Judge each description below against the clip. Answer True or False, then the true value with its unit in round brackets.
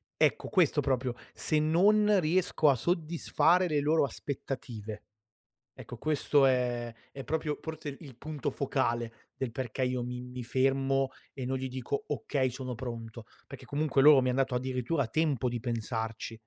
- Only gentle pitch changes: False (3.5 semitones)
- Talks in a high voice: False (135 Hz)